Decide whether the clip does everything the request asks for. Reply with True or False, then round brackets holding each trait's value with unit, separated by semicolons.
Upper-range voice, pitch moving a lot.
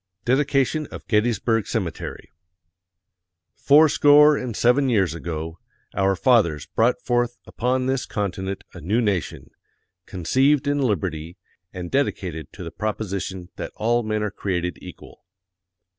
False (110 Hz; 5.8 semitones)